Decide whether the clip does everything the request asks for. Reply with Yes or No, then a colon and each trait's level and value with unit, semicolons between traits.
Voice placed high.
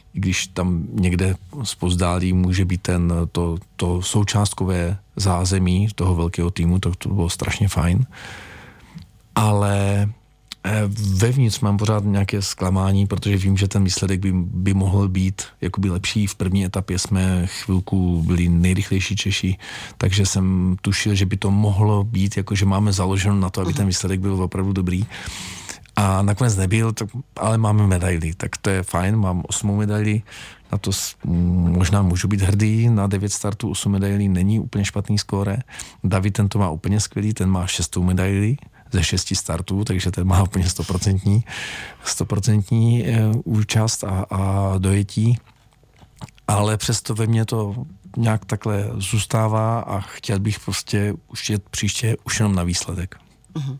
No: low, 100 Hz